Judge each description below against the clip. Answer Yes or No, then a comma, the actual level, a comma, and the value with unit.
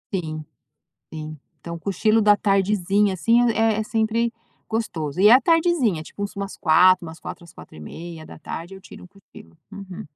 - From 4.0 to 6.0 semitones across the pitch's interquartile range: Yes, average, 4.7 semitones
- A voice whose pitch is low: No, high, 195 Hz